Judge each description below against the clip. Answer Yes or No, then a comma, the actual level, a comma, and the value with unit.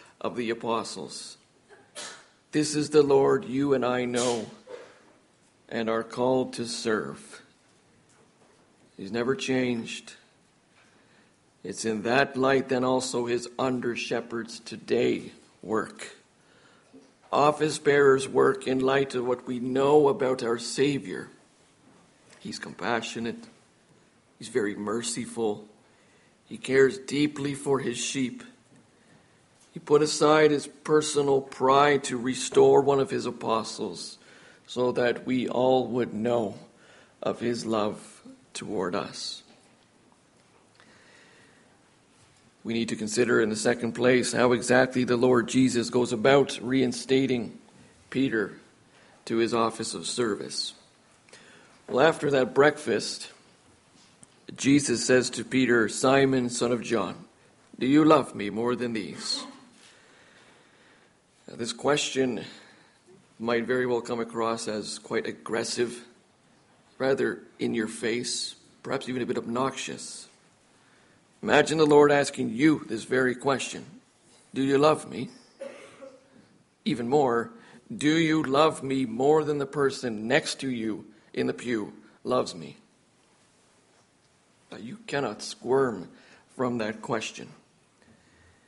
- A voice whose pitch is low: Yes, low, 125 Hz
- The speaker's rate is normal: No, slow, 120 wpm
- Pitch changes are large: No, average, 2.9 semitones